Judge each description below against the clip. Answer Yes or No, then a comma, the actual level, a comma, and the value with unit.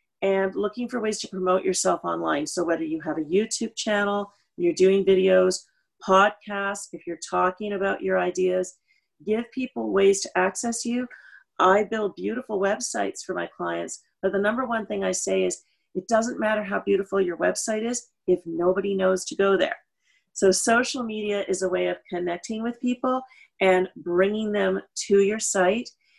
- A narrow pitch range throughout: No, average, 3.3 semitones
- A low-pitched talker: No, high, 195 Hz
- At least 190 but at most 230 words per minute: No, average, 175 wpm